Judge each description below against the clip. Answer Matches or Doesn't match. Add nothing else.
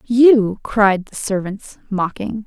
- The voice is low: Doesn't match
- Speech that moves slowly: Matches